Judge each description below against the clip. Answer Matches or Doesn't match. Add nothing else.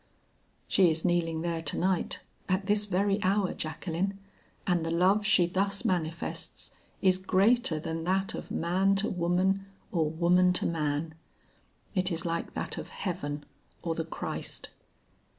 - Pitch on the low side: Doesn't match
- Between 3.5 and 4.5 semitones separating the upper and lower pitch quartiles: Doesn't match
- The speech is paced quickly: Doesn't match